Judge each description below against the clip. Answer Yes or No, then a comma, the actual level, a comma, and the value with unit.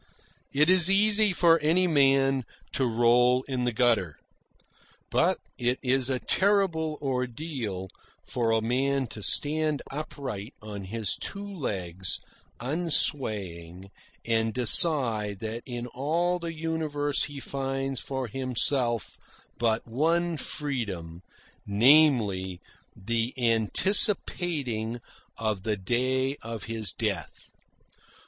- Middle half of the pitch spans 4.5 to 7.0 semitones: Yes, average, 5.2 semitones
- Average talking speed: No, slow, 110 wpm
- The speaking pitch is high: No, low, 130 Hz